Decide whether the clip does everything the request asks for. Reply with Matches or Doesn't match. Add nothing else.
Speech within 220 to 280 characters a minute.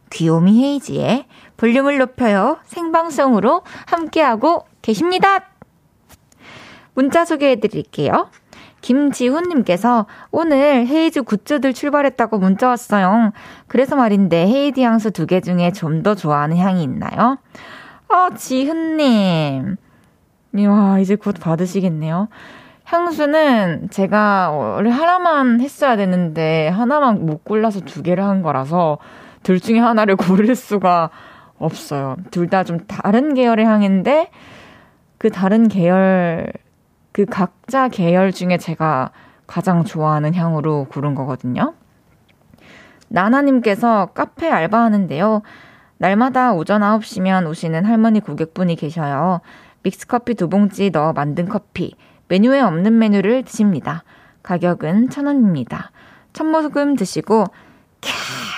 Matches